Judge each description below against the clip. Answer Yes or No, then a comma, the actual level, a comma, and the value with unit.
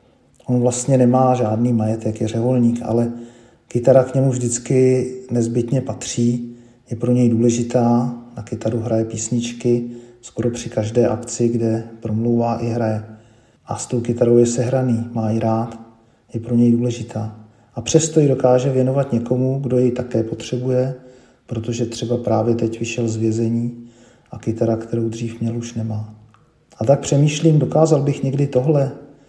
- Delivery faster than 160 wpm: No, average, 150 wpm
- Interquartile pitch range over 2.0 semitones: No, narrow, 1.7 semitones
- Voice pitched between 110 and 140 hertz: Yes, low, 120 Hz